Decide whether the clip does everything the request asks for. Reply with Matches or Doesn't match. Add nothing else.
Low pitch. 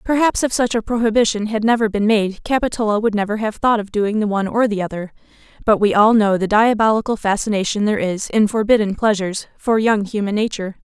Doesn't match